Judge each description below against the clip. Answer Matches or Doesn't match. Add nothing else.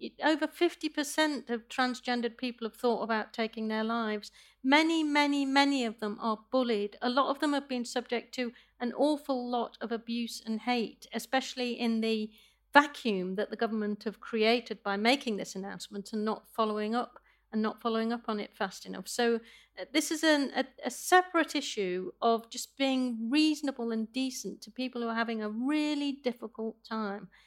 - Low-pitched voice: Doesn't match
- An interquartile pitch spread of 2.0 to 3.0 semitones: Doesn't match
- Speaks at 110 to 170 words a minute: Doesn't match